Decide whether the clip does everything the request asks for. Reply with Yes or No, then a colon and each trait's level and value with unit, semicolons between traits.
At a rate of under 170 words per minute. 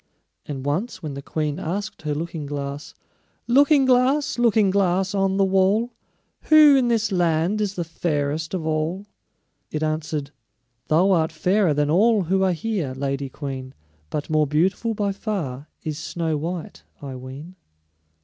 Yes: average, 155 wpm